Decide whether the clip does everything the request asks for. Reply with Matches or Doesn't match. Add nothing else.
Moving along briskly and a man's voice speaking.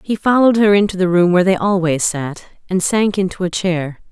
Doesn't match